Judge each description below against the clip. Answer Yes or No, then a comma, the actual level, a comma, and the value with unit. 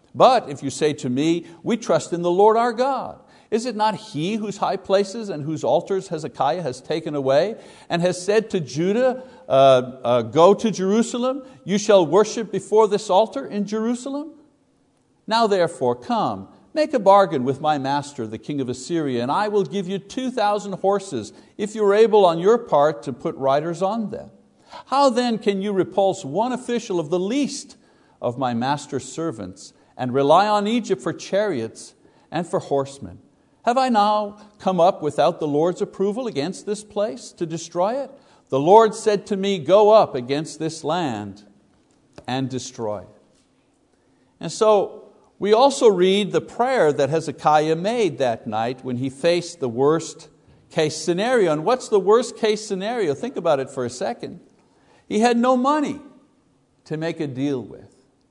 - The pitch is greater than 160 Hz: Yes, high, 190 Hz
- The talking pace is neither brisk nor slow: Yes, average, 175 wpm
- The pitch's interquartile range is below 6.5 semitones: No, wide, 6.8 semitones